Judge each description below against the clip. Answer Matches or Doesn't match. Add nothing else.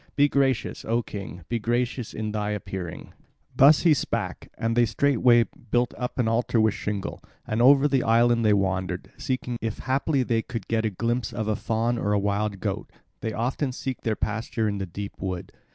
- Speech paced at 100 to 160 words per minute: Doesn't match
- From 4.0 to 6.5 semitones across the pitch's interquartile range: Doesn't match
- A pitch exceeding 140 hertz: Doesn't match